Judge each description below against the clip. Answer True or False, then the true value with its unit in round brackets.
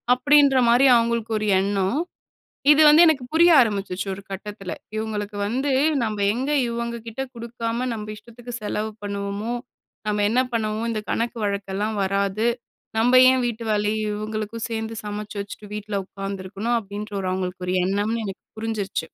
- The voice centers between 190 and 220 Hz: True (215 Hz)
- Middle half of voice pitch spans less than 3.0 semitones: True (2.6 semitones)